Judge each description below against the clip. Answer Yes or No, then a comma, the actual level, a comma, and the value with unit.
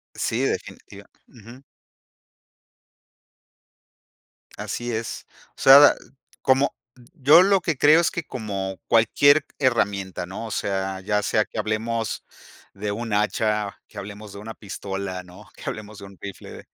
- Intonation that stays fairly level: No, average, 4.3 semitones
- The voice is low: Yes, low, 110 Hz